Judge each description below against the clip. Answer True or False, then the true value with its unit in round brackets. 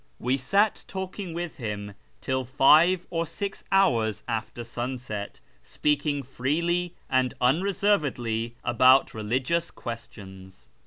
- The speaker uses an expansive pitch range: True (6.6 semitones)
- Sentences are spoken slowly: True (105 wpm)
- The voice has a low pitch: True (130 Hz)